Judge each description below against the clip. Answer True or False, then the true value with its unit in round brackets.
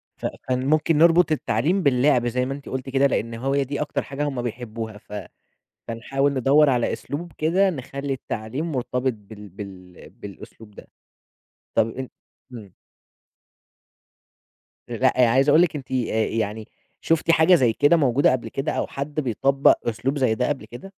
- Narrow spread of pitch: False (4.1 semitones)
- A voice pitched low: True (130 Hz)